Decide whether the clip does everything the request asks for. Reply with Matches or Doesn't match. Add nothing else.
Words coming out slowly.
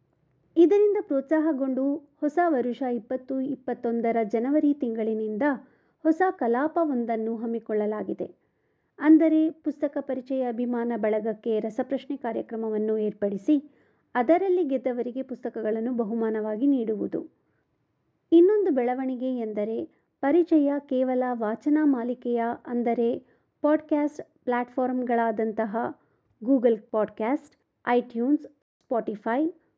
Doesn't match